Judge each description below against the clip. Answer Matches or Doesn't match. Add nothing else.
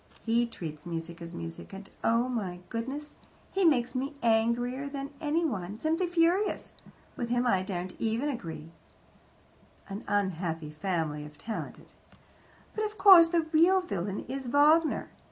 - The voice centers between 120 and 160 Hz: Doesn't match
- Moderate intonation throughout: Doesn't match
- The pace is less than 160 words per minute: Matches